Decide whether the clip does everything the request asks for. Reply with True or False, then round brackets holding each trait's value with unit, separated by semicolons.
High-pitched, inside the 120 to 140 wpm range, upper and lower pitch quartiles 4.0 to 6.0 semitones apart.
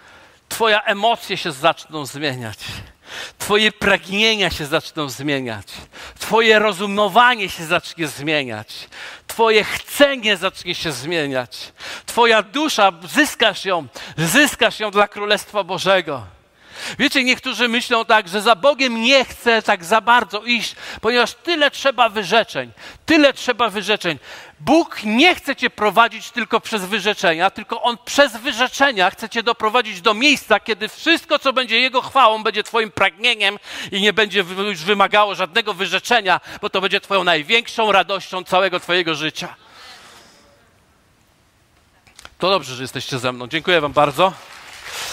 True (210 Hz; 135 wpm; 4.8 semitones)